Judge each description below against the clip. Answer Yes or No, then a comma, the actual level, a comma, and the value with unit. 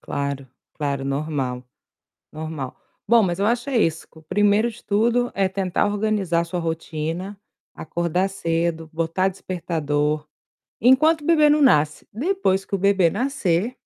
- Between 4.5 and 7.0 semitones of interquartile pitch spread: Yes, average, 5.2 semitones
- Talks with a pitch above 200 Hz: No, medium, 185 Hz